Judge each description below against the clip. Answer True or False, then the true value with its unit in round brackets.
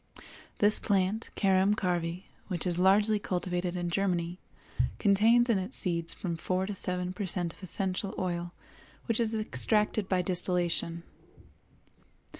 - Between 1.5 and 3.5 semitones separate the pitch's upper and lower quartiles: True (2.6 semitones)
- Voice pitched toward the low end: False (185 Hz)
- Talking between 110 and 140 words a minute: True (135 wpm)